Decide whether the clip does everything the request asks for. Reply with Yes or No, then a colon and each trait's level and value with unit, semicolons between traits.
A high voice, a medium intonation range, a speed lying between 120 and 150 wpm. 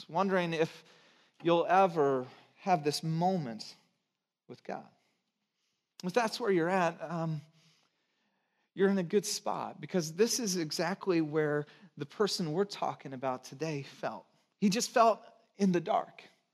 No: medium, 170 Hz; average, 3.6 semitones; average, 140 wpm